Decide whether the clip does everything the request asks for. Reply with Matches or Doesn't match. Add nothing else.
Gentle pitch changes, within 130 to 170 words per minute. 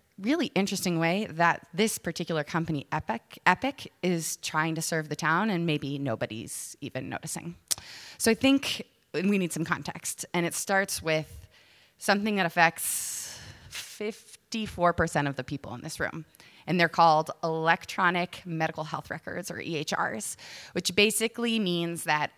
Doesn't match